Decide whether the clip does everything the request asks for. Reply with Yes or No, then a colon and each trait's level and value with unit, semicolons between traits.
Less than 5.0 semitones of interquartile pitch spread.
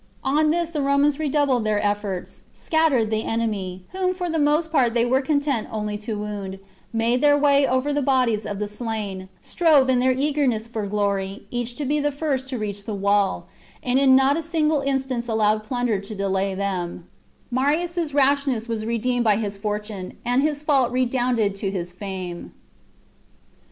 No: average, 5.3 semitones